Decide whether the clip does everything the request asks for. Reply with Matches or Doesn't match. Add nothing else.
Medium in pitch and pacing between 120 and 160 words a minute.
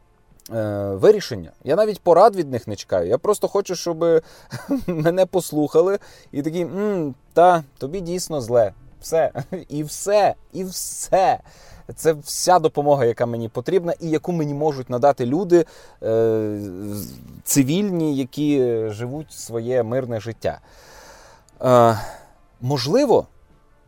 Doesn't match